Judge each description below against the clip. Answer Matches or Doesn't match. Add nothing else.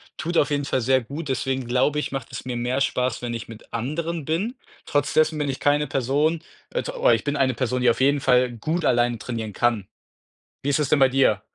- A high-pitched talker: Doesn't match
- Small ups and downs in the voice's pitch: Doesn't match